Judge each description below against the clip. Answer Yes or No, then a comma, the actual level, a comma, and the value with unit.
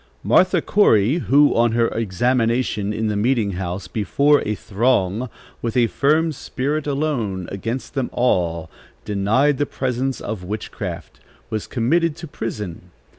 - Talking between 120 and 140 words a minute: Yes, slow, 135 wpm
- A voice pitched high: No, low, 115 Hz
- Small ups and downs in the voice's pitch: No, average, 5.1 semitones